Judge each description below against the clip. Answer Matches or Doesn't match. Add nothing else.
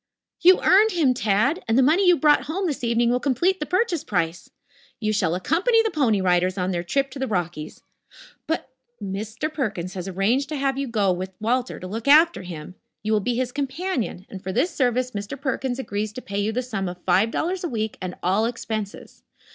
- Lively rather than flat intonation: Matches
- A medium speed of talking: Doesn't match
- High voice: Matches